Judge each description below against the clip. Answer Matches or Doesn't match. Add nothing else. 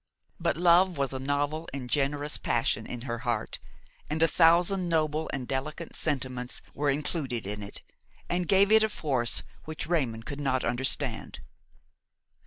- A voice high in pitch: Doesn't match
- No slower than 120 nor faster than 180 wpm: Matches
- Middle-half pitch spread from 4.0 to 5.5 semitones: Matches